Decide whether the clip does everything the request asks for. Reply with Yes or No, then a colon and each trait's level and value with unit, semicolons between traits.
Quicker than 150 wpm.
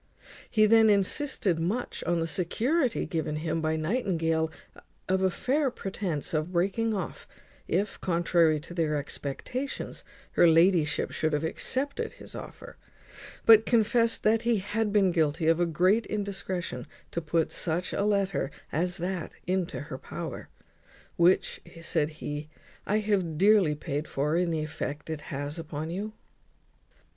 No: average, 145 wpm